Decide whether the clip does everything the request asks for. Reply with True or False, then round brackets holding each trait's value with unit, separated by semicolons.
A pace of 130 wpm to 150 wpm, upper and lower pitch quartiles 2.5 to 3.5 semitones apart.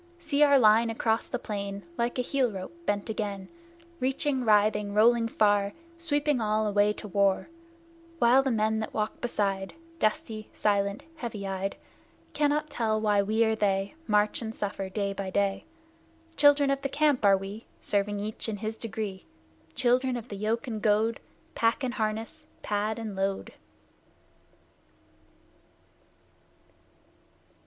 True (145 wpm; 3.0 semitones)